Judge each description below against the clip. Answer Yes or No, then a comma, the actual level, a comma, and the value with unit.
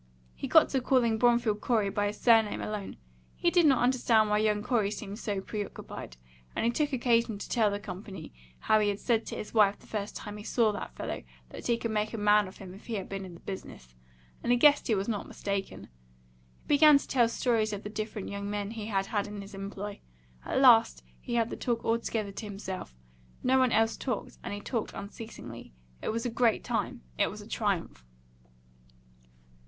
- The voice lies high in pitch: Yes, high, 215 Hz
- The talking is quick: Yes, fast, 215 wpm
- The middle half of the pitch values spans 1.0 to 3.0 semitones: Yes, narrow, 2.6 semitones